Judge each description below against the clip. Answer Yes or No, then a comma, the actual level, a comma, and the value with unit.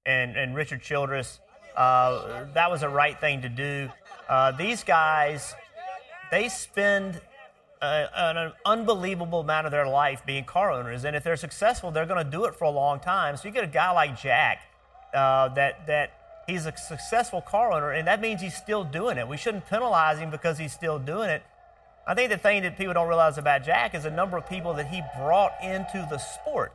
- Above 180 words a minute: Yes, fast, 205 wpm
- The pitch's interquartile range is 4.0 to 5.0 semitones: Yes, average, 4.7 semitones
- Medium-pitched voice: Yes, medium, 160 Hz